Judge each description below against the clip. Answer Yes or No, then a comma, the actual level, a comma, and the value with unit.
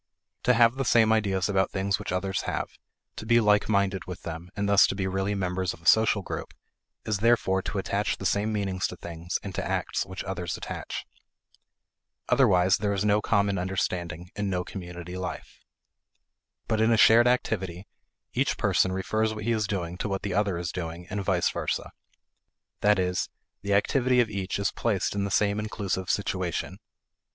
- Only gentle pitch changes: Yes, narrow, 2.3 semitones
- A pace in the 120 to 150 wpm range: No, average, 185 wpm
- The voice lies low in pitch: Yes, low, 100 Hz